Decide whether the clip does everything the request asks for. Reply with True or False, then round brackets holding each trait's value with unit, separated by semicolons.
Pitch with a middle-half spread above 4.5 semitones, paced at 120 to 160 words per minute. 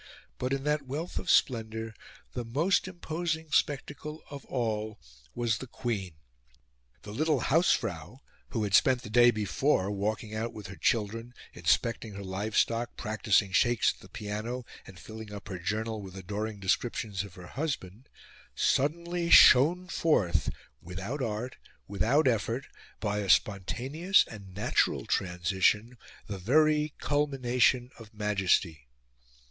True (4.9 semitones; 135 wpm)